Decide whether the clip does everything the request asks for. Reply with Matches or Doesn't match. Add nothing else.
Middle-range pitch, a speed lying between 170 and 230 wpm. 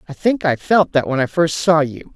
Doesn't match